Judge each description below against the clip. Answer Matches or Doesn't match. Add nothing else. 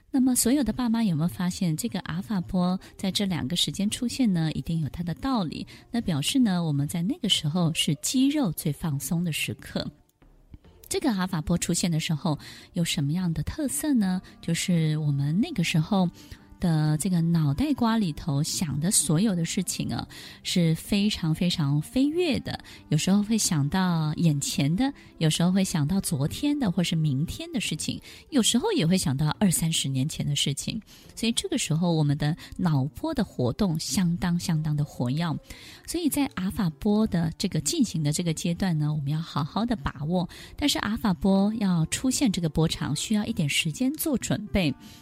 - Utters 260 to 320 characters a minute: Matches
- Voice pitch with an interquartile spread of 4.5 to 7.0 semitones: Matches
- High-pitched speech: Doesn't match